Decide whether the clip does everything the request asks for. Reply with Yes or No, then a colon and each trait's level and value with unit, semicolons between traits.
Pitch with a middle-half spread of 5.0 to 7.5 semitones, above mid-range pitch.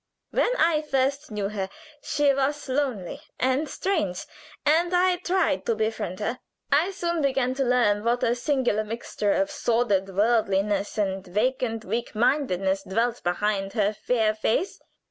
Yes: wide, 5.5 semitones; high, 235 Hz